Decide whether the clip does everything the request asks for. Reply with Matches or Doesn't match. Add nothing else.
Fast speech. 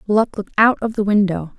Matches